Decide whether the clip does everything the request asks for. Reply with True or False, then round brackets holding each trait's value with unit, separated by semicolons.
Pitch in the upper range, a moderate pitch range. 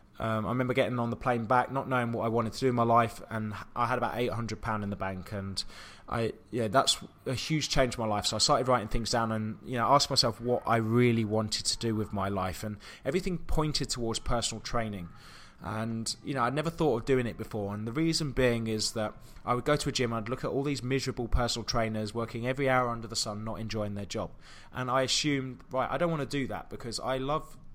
False (115 Hz; 3.1 semitones)